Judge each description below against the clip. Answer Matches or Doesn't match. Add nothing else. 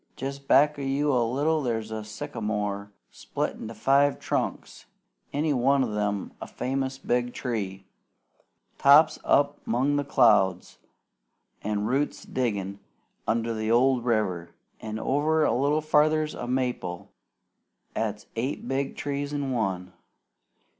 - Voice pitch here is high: Doesn't match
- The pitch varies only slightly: Doesn't match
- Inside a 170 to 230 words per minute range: Doesn't match